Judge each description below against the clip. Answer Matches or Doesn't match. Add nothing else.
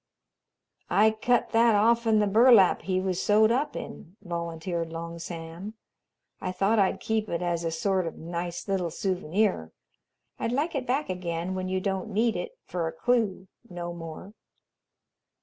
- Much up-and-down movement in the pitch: Doesn't match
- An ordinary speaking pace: Matches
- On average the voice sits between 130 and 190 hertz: Matches